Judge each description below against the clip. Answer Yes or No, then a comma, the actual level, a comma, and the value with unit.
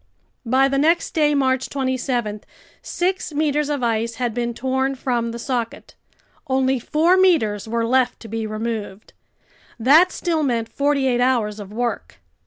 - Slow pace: No, average, 155 wpm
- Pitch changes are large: No, average, 3.6 semitones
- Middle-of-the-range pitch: No, very high, 255 Hz